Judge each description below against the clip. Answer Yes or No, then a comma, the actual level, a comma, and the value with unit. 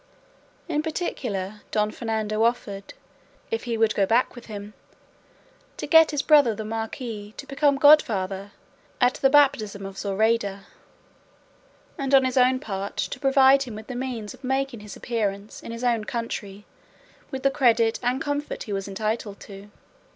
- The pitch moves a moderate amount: Yes, average, 4.3 semitones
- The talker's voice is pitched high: Yes, high, 230 Hz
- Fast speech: No, average, 160 wpm